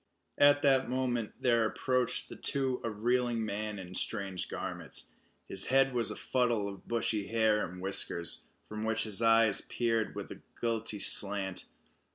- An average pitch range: Yes, average, 3.2 semitones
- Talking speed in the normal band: Yes, average, 160 wpm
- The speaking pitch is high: No, low, 115 Hz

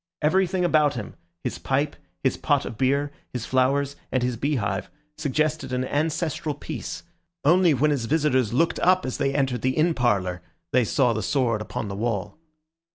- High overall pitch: No, low, 135 Hz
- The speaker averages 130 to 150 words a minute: No, average, 170 wpm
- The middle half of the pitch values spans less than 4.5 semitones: Yes, average, 4.0 semitones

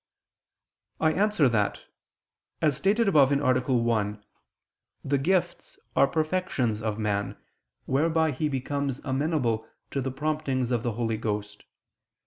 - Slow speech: Yes, slow, 120 wpm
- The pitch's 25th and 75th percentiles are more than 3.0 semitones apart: Yes, wide, 5.4 semitones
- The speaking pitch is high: No, low, 135 Hz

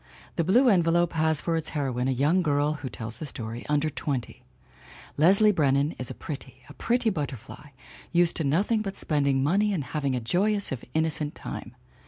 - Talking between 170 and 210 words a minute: Yes, average, 185 wpm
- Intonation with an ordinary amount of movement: Yes, average, 4.3 semitones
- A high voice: No, medium, 150 Hz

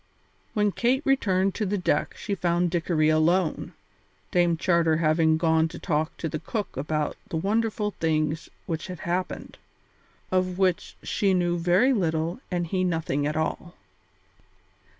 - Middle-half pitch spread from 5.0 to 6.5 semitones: No, average, 2.9 semitones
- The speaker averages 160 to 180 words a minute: No, average, 150 wpm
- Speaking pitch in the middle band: Yes, medium, 175 Hz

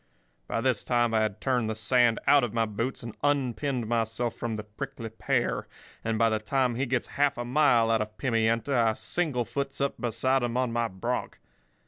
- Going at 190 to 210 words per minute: Yes, average, 195 wpm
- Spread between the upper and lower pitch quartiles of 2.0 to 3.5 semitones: Yes, narrow, 2.5 semitones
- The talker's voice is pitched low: Yes, low, 120 Hz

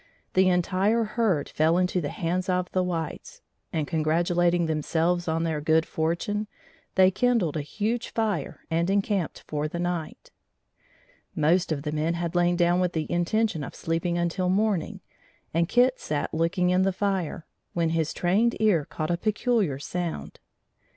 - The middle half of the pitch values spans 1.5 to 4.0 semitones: Yes, average, 2.9 semitones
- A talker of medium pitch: Yes, medium, 175 Hz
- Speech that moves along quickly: No, average, 160 wpm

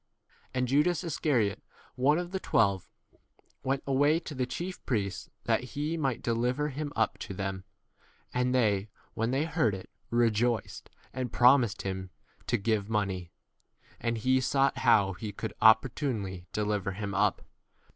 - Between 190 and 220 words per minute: No, average, 155 wpm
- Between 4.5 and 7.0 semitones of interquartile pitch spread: Yes, average, 5.0 semitones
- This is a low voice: Yes, low, 120 Hz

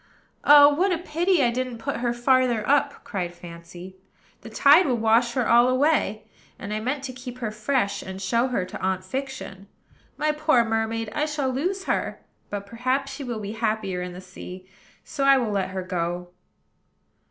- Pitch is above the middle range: Yes, high, 235 Hz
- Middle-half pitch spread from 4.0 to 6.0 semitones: Yes, wide, 5.5 semitones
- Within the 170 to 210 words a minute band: Yes, average, 185 wpm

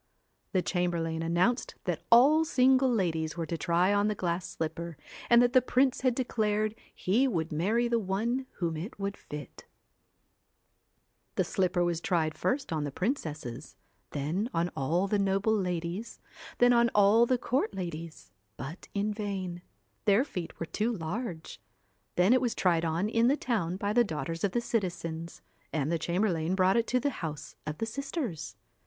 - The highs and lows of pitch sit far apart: Yes, wide, 5.8 semitones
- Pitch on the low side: No, high, 190 Hz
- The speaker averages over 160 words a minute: Yes, average, 170 wpm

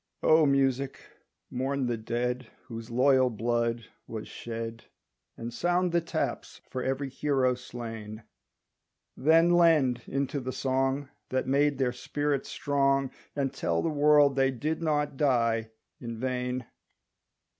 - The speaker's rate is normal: No, slow, 130 wpm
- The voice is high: No, low, 130 Hz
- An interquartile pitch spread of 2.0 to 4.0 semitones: Yes, average, 3.1 semitones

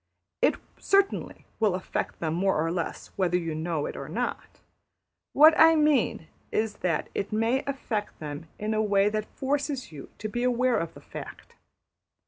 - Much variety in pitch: Yes, wide, 7.0 semitones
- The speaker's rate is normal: Yes, average, 170 wpm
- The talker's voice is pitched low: No, high, 210 Hz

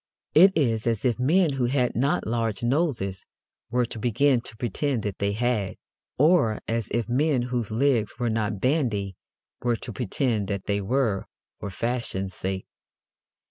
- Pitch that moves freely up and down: No, average, 3.8 semitones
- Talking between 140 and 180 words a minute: Yes, average, 160 wpm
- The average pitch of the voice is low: Yes, low, 120 Hz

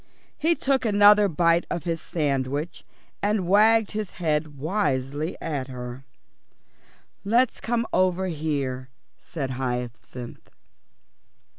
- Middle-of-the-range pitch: Yes, medium, 165 Hz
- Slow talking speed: Yes, slow, 105 wpm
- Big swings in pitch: Yes, wide, 7.2 semitones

